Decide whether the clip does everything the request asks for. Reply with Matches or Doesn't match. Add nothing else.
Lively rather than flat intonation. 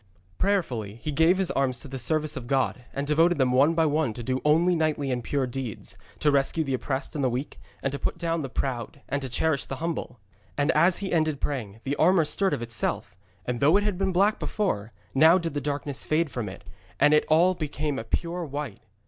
Doesn't match